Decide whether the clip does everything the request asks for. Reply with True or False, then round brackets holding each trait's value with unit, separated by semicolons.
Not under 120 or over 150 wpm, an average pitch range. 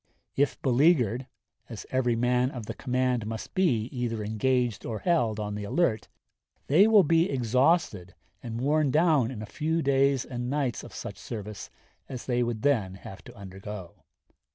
False (165 wpm; 4.2 semitones)